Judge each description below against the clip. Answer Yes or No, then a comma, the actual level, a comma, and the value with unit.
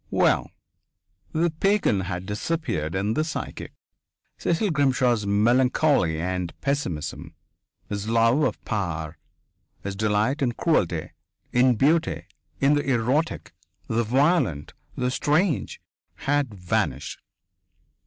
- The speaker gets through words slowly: Yes, slow, 105 wpm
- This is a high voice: No, low, 120 Hz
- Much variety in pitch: Yes, wide, 6.7 semitones